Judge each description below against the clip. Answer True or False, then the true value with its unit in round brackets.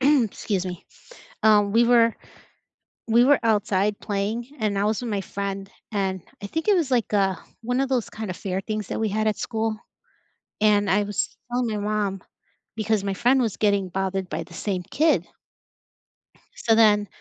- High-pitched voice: True (210 Hz)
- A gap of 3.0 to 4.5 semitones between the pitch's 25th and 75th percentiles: False (2.6 semitones)